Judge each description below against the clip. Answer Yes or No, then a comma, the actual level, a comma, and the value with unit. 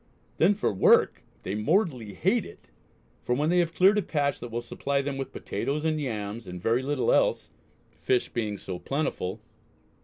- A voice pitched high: No, low, 135 Hz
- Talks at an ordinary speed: Yes, average, 180 wpm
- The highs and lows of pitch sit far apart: Yes, wide, 6.0 semitones